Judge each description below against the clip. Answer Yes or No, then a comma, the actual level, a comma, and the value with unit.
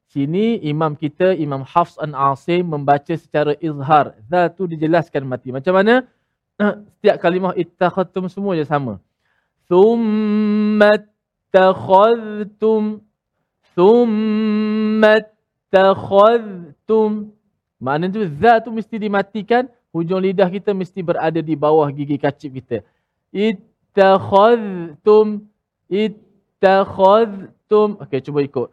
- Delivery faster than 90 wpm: Yes, average, 100 wpm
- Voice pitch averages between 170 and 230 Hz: Yes, high, 190 Hz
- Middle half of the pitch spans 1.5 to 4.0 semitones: No, average, 5.3 semitones